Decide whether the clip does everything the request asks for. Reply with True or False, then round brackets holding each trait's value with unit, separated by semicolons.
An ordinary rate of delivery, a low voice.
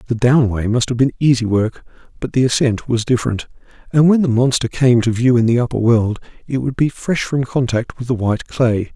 False (220 wpm; 120 Hz)